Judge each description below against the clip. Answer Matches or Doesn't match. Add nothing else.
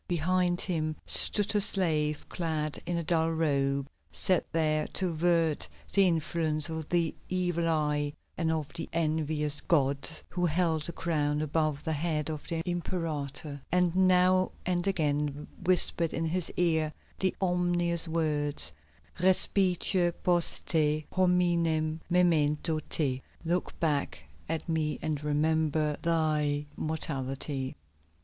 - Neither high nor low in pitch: Matches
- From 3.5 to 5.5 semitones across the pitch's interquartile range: Doesn't match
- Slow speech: Matches